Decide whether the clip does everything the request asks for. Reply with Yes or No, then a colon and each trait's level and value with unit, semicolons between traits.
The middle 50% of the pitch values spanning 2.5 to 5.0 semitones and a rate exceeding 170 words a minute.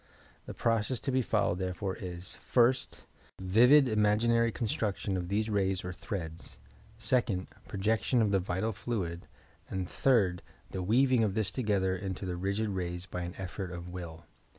No: average, 3.7 semitones; average, 155 wpm